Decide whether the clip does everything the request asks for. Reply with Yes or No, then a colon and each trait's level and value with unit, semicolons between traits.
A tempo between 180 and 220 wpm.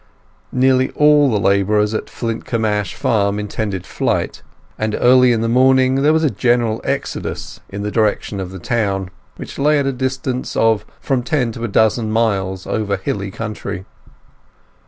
No: average, 165 wpm